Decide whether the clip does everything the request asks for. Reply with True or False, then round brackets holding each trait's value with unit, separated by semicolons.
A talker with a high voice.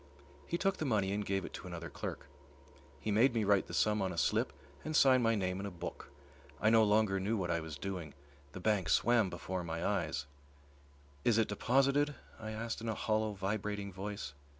False (105 Hz)